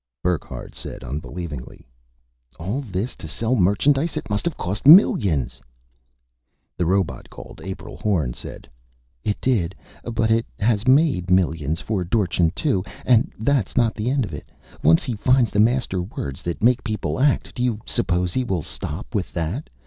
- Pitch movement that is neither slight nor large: No, wide, 5.7 semitones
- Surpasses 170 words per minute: No, average, 165 wpm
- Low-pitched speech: Yes, low, 105 Hz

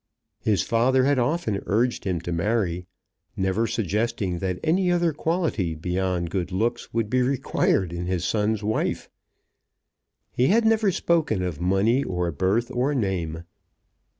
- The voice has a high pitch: No, low, 105 Hz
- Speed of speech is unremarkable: Yes, average, 145 wpm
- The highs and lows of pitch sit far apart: Yes, wide, 5.9 semitones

